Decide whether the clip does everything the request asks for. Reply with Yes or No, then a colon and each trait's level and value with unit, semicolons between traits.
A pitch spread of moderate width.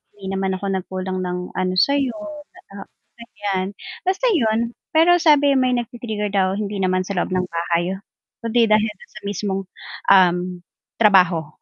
Yes: average, 4.0 semitones